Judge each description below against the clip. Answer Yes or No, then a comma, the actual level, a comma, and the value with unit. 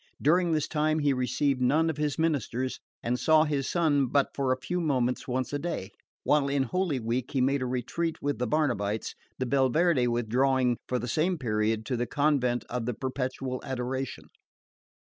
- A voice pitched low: Yes, low, 130 Hz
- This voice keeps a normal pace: Yes, average, 185 wpm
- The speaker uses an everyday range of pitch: Yes, average, 3.3 semitones